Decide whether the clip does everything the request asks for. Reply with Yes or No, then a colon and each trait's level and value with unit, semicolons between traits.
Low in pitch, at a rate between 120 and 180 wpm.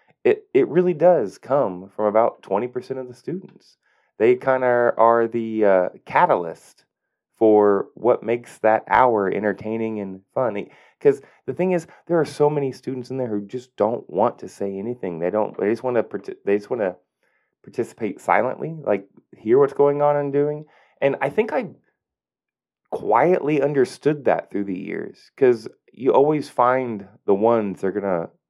Yes: low, 130 Hz; average, 175 wpm